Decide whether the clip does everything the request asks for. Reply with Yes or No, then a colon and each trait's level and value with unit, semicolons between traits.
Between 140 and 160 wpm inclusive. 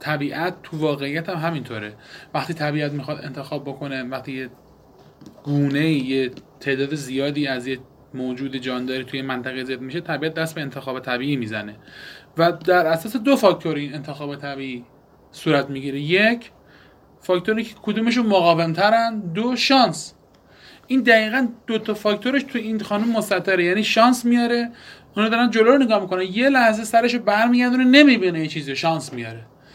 Yes: average, 150 wpm